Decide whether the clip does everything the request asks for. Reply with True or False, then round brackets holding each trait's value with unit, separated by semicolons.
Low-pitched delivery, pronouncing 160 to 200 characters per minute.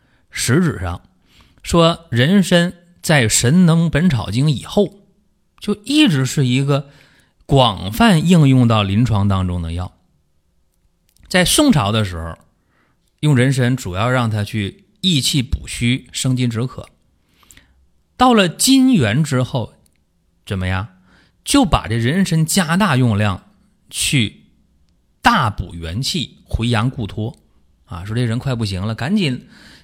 True (125 Hz; 180 characters per minute)